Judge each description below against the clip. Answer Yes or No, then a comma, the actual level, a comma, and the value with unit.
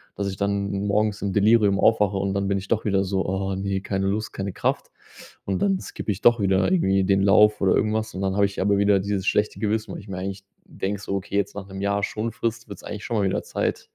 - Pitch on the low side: Yes, low, 100 Hz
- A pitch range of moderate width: No, narrow, 1.3 semitones